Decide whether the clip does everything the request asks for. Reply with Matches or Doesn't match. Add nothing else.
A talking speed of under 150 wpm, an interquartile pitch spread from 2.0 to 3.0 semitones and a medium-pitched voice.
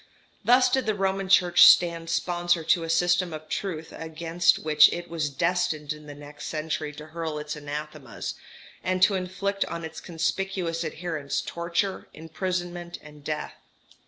Doesn't match